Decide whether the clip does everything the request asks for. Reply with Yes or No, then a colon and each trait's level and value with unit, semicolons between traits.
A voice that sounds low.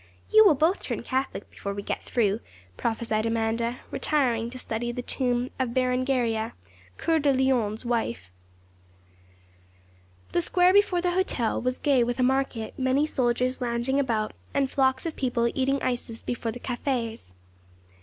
No: very high, 250 Hz